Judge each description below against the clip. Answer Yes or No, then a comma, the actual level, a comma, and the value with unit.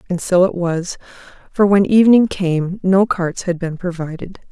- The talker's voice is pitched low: No, medium, 180 Hz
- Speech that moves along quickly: No, average, 175 wpm